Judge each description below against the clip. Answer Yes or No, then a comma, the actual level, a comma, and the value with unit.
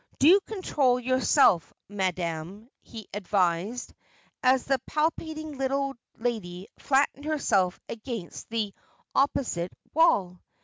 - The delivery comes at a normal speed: No, slow, 95 wpm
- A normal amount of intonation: No, wide, 6.7 semitones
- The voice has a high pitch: Yes, high, 240 Hz